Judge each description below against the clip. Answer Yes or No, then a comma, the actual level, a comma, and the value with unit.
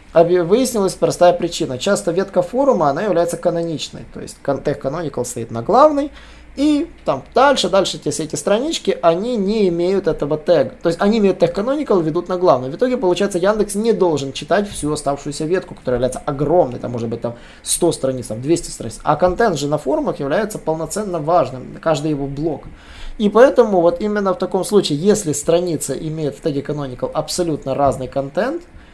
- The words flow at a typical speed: No, fast, 175 wpm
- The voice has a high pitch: No, medium, 170 Hz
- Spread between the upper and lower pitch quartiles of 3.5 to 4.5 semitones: No, average, 5.1 semitones